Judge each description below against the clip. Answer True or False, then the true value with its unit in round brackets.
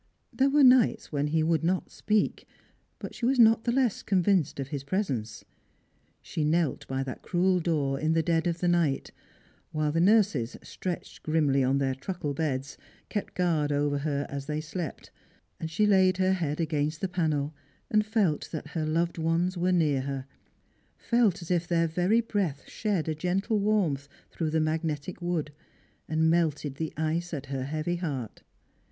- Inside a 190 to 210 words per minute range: False (180 wpm)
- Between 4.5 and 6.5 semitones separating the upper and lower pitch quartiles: False (3.9 semitones)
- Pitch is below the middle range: False (160 Hz)